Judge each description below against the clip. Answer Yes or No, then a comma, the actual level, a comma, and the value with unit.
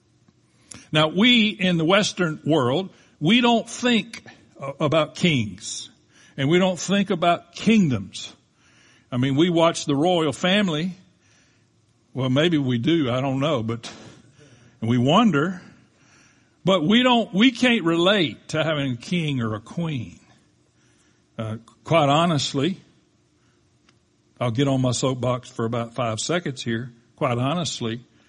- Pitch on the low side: No, medium, 145 Hz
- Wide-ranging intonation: Yes, wide, 6.6 semitones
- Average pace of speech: No, slow, 130 wpm